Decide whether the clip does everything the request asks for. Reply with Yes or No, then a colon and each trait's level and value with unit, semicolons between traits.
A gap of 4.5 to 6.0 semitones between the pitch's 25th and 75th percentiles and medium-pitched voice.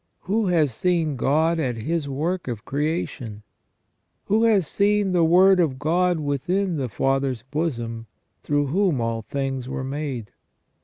Yes: average, 5.3 semitones; medium, 150 Hz